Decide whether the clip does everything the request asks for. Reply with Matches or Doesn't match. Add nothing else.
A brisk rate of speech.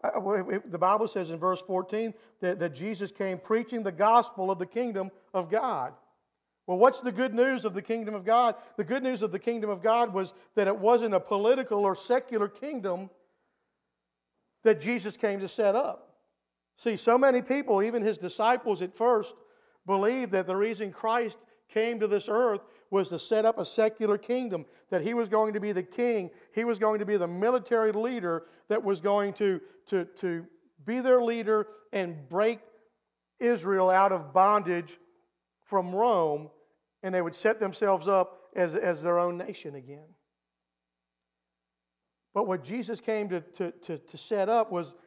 Doesn't match